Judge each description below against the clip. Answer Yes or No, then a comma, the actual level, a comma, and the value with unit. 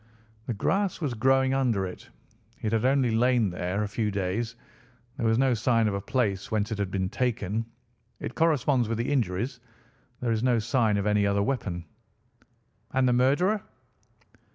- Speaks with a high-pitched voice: No, low, 115 Hz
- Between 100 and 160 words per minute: No, average, 175 wpm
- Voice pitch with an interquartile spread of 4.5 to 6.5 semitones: No, average, 4.0 semitones